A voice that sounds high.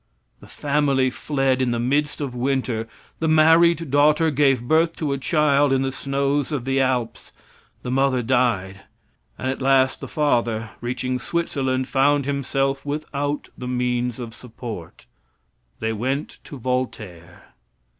No: low, 135 Hz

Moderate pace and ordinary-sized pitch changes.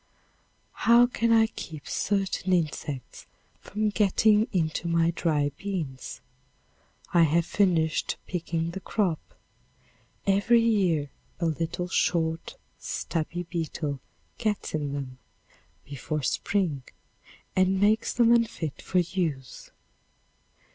No: slow, 105 wpm; average, 4.5 semitones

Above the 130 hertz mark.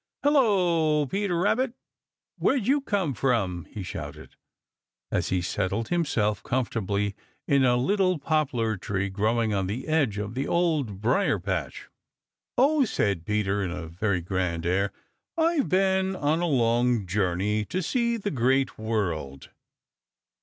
No: low, 120 Hz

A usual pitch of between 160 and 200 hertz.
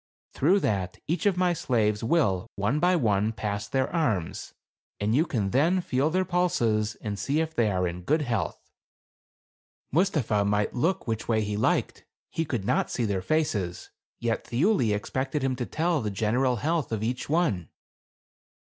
No: low, 120 Hz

